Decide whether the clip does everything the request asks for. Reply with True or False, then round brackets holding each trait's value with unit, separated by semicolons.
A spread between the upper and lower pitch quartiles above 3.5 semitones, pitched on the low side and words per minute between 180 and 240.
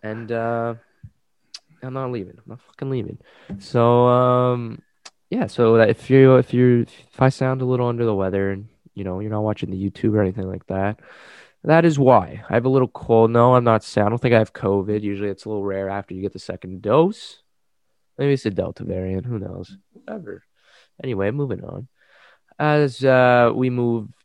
True (4.1 semitones; 115 Hz; 200 wpm)